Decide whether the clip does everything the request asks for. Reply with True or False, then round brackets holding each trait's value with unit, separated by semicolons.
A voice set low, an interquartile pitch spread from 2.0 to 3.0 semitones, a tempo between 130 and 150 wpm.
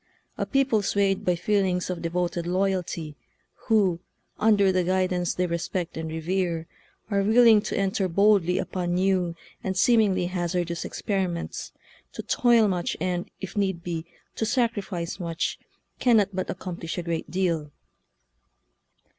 False (185 Hz; 2.5 semitones; 140 wpm)